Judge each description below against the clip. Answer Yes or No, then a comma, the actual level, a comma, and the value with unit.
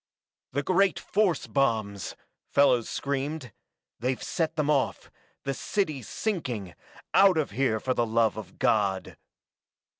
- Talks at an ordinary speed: No, slow, 125 wpm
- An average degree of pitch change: No, wide, 6.0 semitones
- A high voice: No, low, 135 Hz